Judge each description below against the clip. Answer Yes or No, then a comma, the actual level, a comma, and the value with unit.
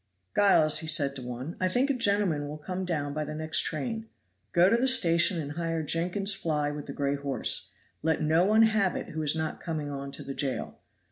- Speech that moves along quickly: Yes, fast, 220 wpm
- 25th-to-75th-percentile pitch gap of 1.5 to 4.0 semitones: No, average, 4.5 semitones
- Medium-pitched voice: Yes, medium, 160 Hz